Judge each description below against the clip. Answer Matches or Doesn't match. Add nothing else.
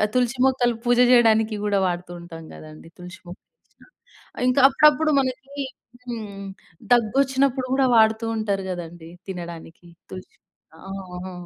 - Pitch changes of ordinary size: Doesn't match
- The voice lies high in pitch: Matches